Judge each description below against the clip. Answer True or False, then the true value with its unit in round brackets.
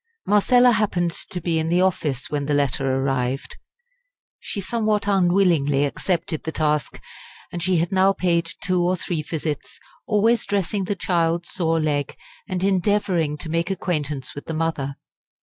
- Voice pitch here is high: False (170 Hz)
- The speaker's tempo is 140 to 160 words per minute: True (155 wpm)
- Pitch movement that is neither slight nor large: True (4.2 semitones)